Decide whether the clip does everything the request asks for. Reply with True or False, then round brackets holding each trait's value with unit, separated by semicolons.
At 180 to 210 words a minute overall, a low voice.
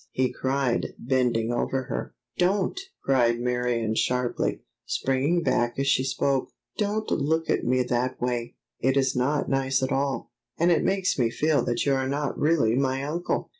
False (170 wpm; 130 Hz)